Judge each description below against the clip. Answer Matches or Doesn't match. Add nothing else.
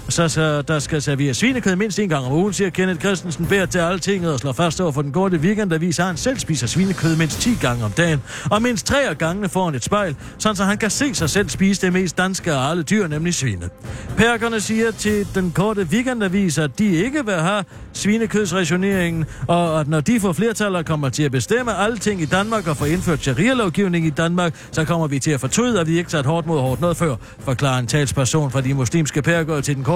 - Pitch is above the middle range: Doesn't match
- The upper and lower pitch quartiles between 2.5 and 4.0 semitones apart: Doesn't match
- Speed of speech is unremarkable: Doesn't match